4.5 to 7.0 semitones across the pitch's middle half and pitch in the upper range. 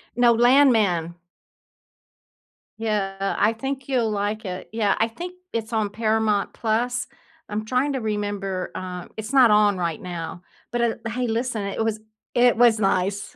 No: average, 3.1 semitones; high, 220 Hz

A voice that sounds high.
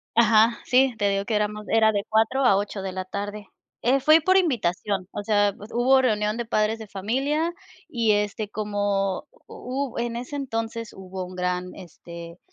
Yes: high, 215 Hz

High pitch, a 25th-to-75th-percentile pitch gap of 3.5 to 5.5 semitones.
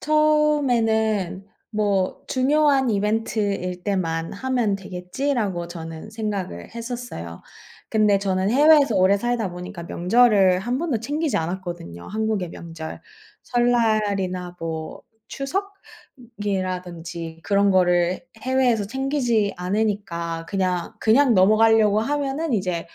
Yes: high, 205 Hz; average, 5.2 semitones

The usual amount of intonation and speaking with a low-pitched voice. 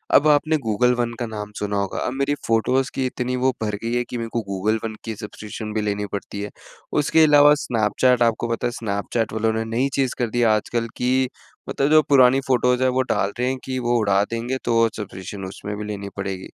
Yes: average, 3.4 semitones; low, 115 Hz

